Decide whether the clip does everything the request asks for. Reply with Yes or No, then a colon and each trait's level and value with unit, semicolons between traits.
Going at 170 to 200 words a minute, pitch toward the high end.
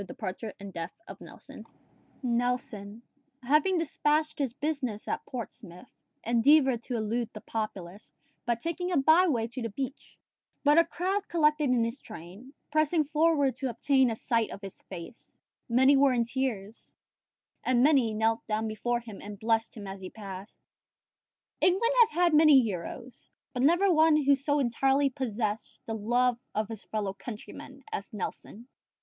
No: average, 160 wpm; high, 245 Hz